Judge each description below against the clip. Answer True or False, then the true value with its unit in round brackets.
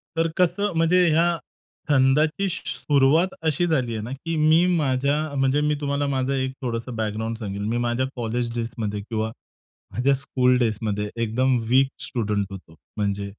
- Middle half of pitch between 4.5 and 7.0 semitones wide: True (5.0 semitones)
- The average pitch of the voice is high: False (130 Hz)